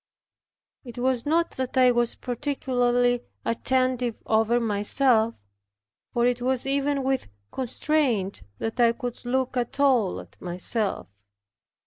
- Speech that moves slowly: Yes, slow, 120 wpm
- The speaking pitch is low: No, high, 245 Hz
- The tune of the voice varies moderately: No, narrow, 2.1 semitones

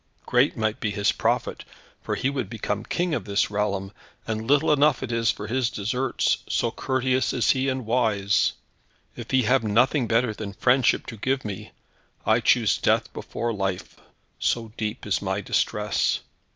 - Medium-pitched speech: No, low, 115 Hz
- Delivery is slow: No, average, 170 wpm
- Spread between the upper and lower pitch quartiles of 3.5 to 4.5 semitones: Yes, average, 3.9 semitones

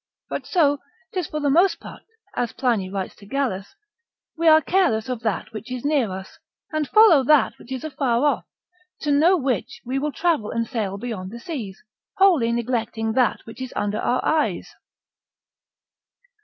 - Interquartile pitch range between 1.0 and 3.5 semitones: No, wide, 5.4 semitones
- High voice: Yes, very high, 255 Hz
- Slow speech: No, average, 170 wpm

